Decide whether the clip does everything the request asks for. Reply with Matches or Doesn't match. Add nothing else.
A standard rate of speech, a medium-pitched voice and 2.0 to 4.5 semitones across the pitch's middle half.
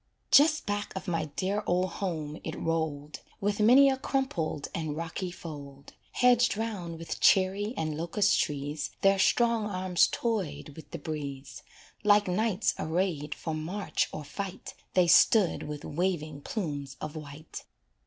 Doesn't match